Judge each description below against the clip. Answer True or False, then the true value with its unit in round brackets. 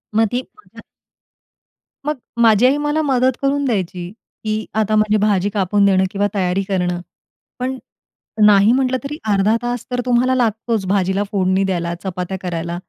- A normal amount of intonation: True (4.6 semitones)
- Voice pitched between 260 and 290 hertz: False (210 Hz)